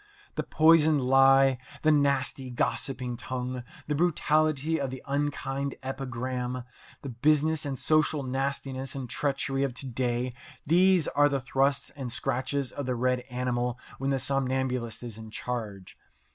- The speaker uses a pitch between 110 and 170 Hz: Yes, low, 135 Hz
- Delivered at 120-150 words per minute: Yes, average, 145 wpm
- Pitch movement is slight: Yes, narrow, 2.1 semitones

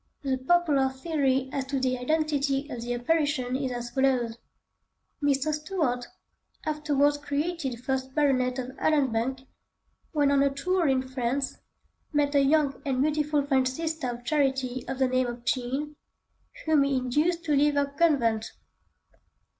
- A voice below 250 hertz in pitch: No, very high, 275 Hz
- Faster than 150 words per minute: No, average, 145 wpm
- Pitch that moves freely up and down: No, narrow, 2.6 semitones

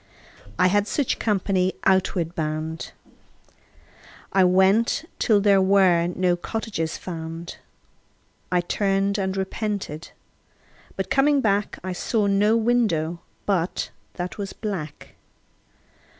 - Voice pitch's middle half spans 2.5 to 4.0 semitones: Yes, average, 2.9 semitones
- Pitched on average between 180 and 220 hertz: Yes, high, 190 Hz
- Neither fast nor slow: No, slow, 105 wpm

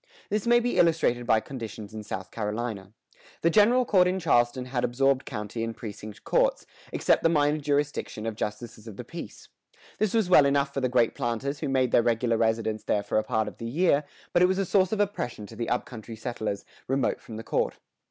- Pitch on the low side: Yes, low, 120 Hz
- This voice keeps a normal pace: No, fast, 215 wpm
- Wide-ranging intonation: Yes, wide, 6.6 semitones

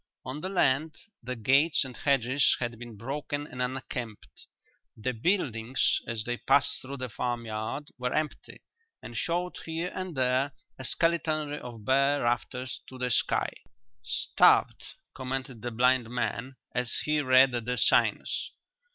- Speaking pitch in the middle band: No, low, 130 Hz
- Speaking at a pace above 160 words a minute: No, average, 145 wpm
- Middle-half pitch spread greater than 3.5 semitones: No, average, 3.0 semitones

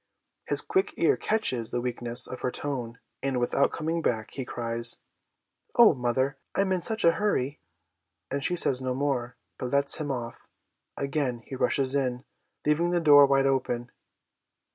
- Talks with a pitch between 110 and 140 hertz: Yes, low, 135 Hz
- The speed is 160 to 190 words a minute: Yes, average, 165 wpm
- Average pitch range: Yes, average, 3.5 semitones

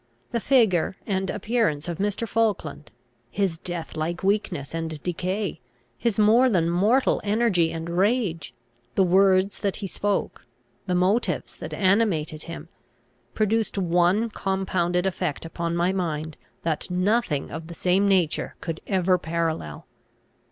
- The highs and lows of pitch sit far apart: No, average, 3.5 semitones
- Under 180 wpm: Yes, slow, 135 wpm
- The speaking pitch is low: No, medium, 185 Hz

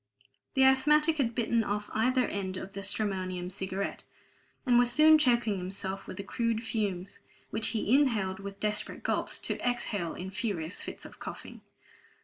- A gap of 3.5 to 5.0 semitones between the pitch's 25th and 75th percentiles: Yes, average, 4.2 semitones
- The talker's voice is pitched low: No, high, 210 Hz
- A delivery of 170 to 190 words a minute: No, average, 160 wpm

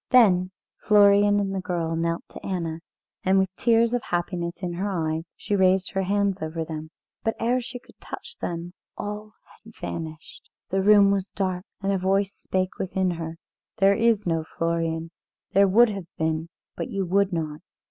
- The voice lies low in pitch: No, high, 190 Hz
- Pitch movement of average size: Yes, average, 3.2 semitones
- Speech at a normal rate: Yes, average, 180 wpm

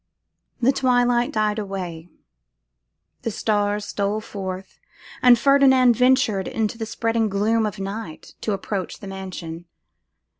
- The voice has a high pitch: Yes, high, 215 Hz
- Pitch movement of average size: Yes, average, 3.6 semitones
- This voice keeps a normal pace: No, slow, 120 wpm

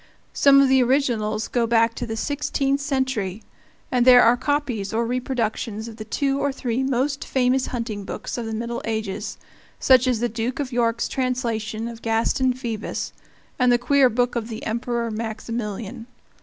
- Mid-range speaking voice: No, high, 240 Hz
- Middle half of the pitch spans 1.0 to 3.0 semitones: Yes, narrow, 2.6 semitones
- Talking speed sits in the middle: Yes, average, 170 wpm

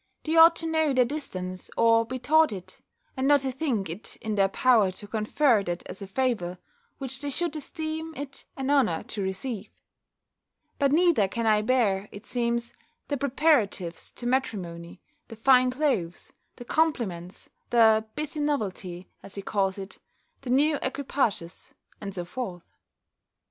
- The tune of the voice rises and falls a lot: Yes, wide, 6.4 semitones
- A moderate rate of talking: Yes, average, 160 wpm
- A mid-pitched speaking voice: No, high, 235 Hz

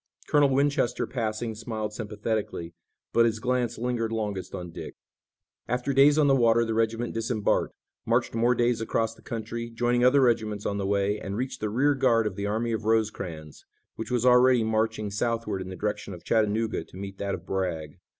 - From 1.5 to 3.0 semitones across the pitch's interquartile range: Yes, average, 2.7 semitones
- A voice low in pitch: Yes, low, 115 Hz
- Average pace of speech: Yes, average, 190 wpm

